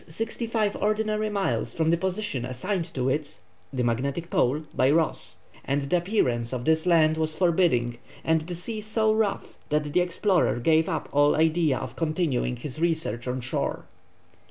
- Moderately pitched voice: Yes, medium, 160 Hz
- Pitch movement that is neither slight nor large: No, wide, 5.7 semitones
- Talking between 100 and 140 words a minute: No, average, 170 wpm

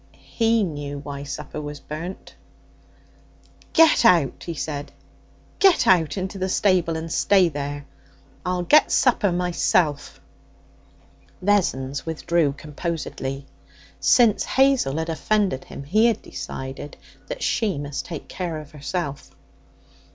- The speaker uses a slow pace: Yes, slow, 120 wpm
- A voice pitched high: No, medium, 165 Hz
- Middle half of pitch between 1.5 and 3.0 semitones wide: No, average, 5.0 semitones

